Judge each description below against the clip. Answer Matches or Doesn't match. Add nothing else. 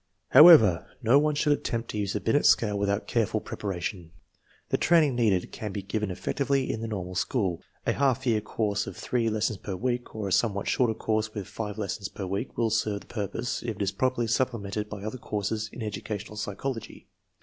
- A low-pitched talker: Matches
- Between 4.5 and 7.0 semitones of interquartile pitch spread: Doesn't match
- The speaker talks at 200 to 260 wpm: Matches